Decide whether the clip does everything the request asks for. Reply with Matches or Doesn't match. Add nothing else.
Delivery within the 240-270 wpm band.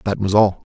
Matches